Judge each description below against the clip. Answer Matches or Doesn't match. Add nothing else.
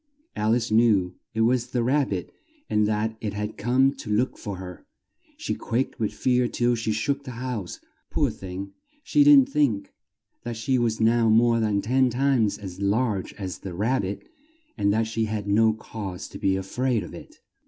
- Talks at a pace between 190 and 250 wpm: Matches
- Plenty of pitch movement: Doesn't match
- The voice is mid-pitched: Doesn't match